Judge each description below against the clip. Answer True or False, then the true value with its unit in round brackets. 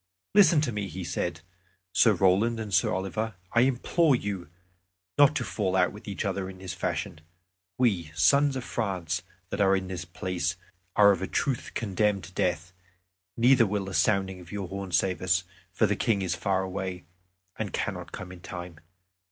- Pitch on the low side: True (95 Hz)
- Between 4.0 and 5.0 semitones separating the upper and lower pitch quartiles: False (3.3 semitones)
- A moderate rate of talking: True (185 wpm)